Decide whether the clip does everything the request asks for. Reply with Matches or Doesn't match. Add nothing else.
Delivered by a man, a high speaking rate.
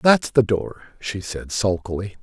Doesn't match